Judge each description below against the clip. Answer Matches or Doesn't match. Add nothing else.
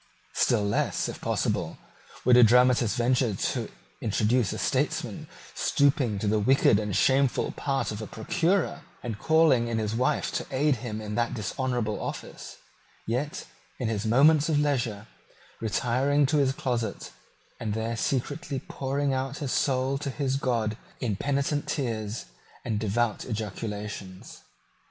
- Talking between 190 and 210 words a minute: Doesn't match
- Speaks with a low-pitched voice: Matches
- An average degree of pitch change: Matches